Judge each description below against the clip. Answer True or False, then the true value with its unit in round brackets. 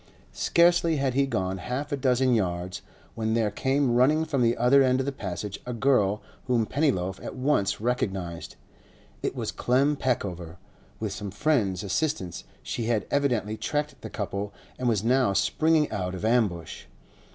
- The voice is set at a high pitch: False (120 Hz)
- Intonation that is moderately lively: False (5.8 semitones)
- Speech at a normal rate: True (165 wpm)